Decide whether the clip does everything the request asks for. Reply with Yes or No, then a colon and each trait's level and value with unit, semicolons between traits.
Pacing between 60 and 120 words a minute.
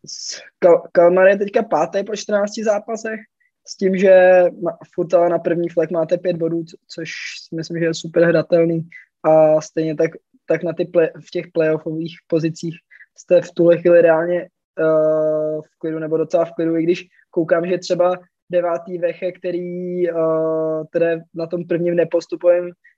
No: average, 165 wpm